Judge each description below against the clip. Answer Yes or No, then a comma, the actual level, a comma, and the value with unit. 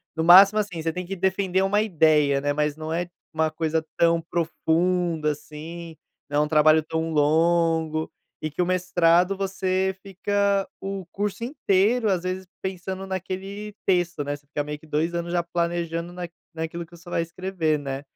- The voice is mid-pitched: Yes, medium, 170 Hz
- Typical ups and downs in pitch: Yes, average, 3.0 semitones